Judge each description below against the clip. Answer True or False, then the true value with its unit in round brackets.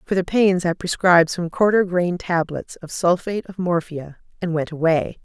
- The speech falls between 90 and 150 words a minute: False (185 wpm)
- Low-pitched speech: False (175 Hz)